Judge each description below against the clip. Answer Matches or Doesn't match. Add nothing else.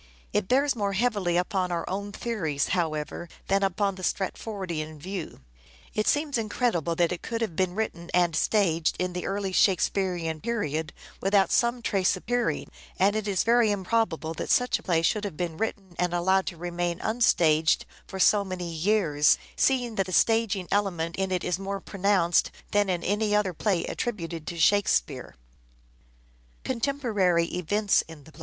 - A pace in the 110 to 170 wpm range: Matches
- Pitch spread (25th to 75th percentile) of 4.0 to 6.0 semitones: Doesn't match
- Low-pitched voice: Doesn't match